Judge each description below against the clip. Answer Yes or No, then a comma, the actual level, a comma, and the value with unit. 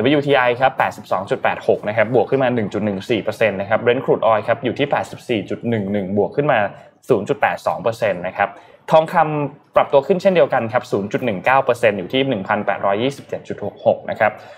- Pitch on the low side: Yes, low, 125 Hz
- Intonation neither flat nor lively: No, wide, 5.7 semitones